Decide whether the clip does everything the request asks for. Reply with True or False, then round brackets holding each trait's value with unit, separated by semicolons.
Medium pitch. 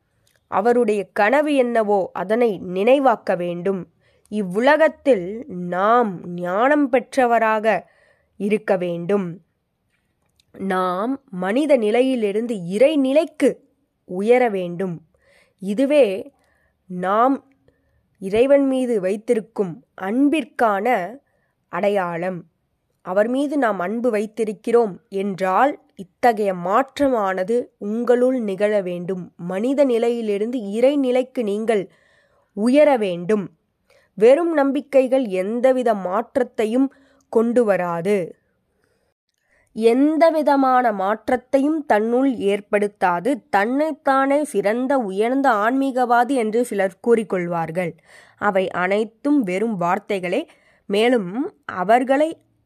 False (225 Hz)